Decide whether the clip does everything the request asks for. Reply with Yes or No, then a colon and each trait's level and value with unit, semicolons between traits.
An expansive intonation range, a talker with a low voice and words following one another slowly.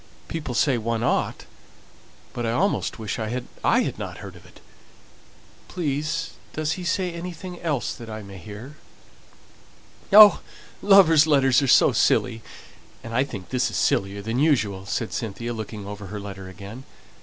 No: wide, 6.3 semitones; low, 120 Hz; average, 150 wpm